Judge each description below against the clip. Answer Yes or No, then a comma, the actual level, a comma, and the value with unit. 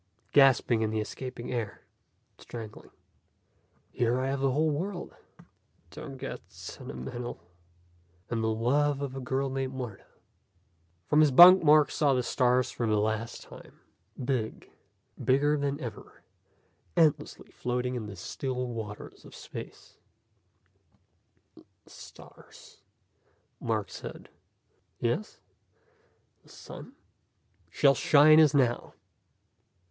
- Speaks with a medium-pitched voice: No, low, 130 Hz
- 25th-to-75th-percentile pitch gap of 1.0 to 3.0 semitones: No, average, 3.7 semitones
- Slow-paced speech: Yes, slow, 120 wpm